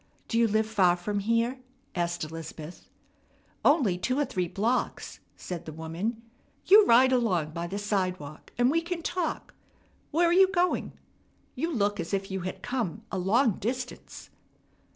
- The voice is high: Yes, high, 215 Hz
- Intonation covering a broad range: Yes, wide, 6.3 semitones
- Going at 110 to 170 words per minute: Yes, average, 160 wpm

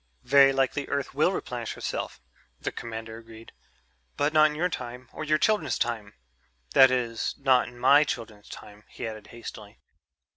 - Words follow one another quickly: No, average, 160 wpm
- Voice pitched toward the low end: Yes, low, 125 Hz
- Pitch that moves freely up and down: No, average, 3.9 semitones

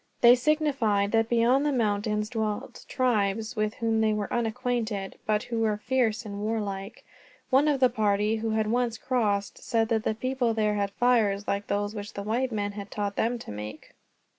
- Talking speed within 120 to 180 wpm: No, average, 190 wpm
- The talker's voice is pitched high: Yes, high, 220 Hz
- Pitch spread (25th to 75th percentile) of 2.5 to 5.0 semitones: Yes, average, 2.8 semitones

